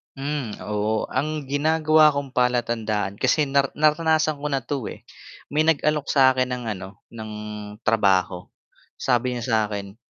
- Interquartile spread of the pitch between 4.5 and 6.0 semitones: Yes, average, 5.1 semitones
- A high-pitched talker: No, low, 130 Hz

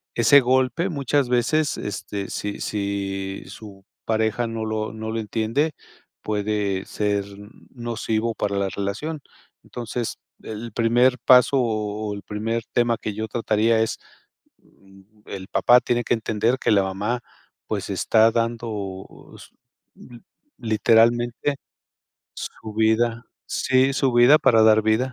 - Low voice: Yes, low, 110 Hz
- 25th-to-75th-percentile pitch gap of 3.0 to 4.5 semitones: No, narrow, 2.5 semitones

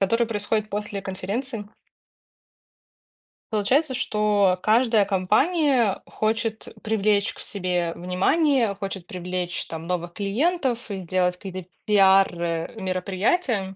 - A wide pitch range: No, average, 3.6 semitones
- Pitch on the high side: Yes, high, 200 Hz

